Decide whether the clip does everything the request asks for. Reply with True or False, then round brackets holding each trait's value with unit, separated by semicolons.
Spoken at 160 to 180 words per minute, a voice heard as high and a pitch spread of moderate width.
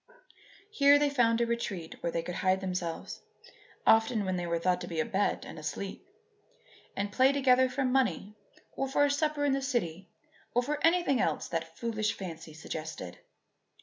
False (175 wpm; 220 Hz; 7.2 semitones)